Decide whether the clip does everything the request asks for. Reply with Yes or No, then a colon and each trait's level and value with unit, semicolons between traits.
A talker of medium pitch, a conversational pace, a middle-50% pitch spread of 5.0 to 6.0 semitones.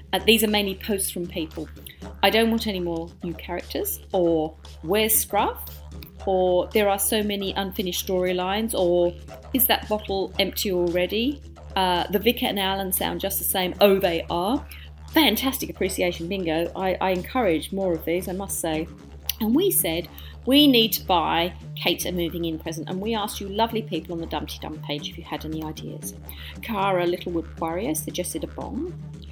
No: medium, 180 Hz; average, 180 wpm; average, 4.0 semitones